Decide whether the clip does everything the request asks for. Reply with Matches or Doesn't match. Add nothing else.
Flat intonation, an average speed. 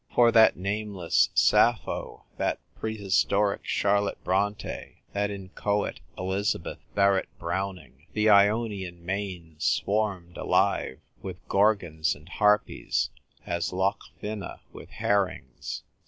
Doesn't match